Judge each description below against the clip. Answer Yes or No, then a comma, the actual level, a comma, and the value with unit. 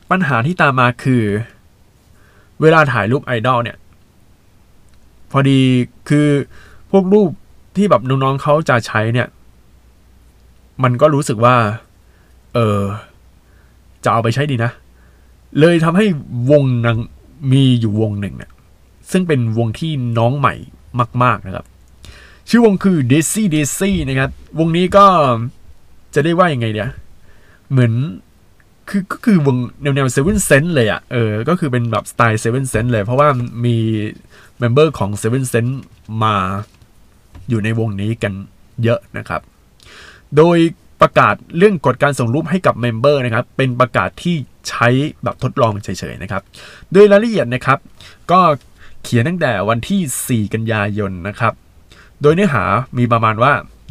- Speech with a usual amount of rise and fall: No, wide, 5.7 semitones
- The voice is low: Yes, low, 120 Hz